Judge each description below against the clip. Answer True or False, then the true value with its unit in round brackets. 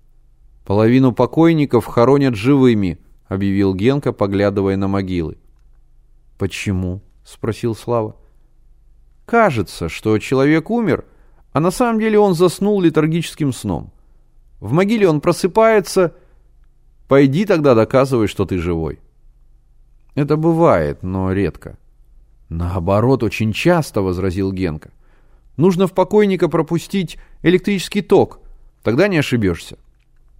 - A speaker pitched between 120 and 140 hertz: True (130 Hz)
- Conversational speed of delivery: False (105 wpm)